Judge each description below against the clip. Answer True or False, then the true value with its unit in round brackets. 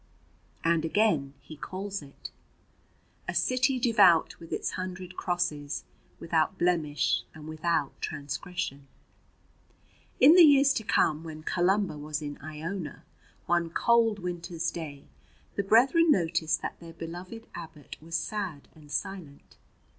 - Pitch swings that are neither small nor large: True (4.3 semitones)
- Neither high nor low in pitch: True (170 Hz)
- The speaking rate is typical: False (125 wpm)